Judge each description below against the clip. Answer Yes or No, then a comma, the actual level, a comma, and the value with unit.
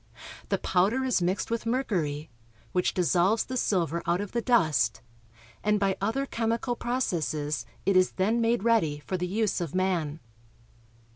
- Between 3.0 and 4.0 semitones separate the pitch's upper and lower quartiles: No, average, 5.0 semitones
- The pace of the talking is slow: No, average, 155 wpm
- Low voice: No, high, 190 Hz